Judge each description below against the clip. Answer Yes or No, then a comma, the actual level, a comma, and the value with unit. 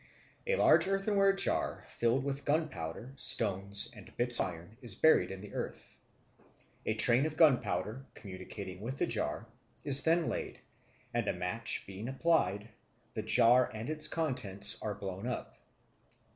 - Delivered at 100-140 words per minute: No, average, 150 wpm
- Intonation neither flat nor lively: No, wide, 6.9 semitones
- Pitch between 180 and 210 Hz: No, low, 120 Hz